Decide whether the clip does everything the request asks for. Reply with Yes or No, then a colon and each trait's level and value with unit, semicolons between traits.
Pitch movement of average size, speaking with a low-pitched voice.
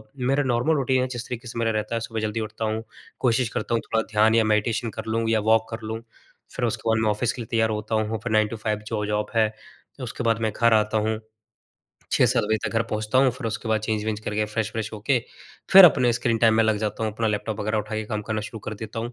No: narrow, 1.4 semitones; low, 110 Hz